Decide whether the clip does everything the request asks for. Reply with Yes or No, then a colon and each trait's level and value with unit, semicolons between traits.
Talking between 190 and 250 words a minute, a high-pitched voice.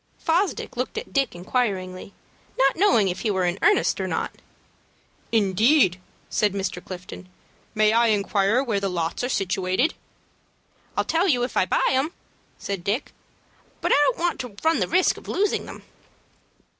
No: average, 165 wpm; high, 215 Hz